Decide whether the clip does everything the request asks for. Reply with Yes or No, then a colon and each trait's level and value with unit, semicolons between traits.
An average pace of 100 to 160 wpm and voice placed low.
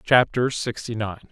Yes: slow, 135 wpm; low, 115 Hz